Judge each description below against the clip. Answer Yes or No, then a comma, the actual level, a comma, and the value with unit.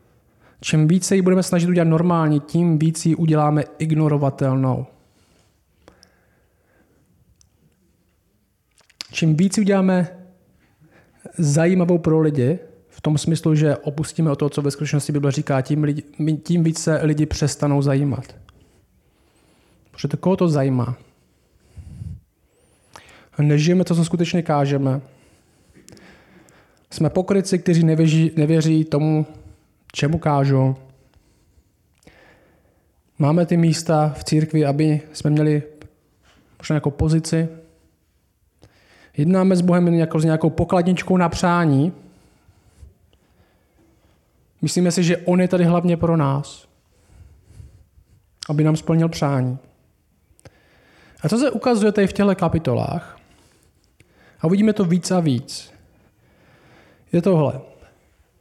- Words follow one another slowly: Yes, slow, 110 wpm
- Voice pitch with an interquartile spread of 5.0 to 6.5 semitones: Yes, wide, 5.5 semitones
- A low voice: No, medium, 150 Hz